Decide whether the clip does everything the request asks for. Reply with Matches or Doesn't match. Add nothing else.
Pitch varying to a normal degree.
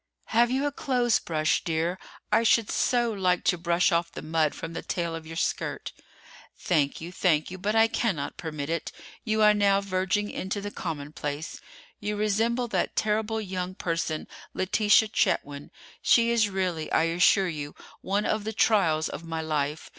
Matches